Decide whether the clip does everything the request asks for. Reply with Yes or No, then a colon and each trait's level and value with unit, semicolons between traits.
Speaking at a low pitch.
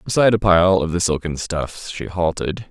Yes: very low, 90 Hz